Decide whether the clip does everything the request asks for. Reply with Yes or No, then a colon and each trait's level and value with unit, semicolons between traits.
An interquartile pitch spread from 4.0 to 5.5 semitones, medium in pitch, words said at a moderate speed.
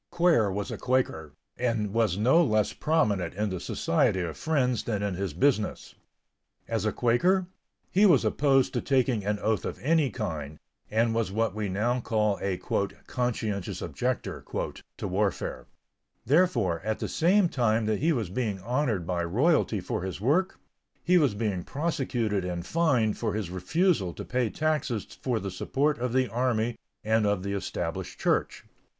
No: average, 4.9 semitones; low, 110 Hz; average, 165 wpm